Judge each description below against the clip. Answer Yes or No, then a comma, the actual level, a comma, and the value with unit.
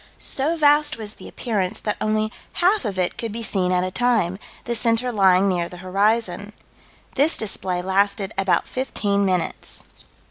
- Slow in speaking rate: No, average, 165 wpm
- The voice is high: Yes, high, 205 Hz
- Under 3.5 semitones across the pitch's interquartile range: No, average, 4.0 semitones